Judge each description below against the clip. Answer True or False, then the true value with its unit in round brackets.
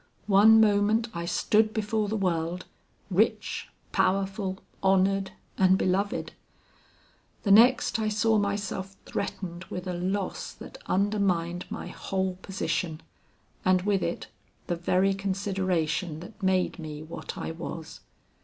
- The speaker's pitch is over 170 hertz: True (190 Hz)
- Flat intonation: True (2.3 semitones)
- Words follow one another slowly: True (125 wpm)